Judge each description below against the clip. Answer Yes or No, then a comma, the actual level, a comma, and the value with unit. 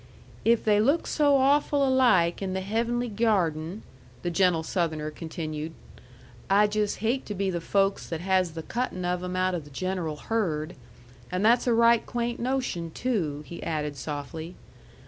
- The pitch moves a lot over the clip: Yes, wide, 5.9 semitones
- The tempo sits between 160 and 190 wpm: Yes, average, 165 wpm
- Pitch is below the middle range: No, high, 190 Hz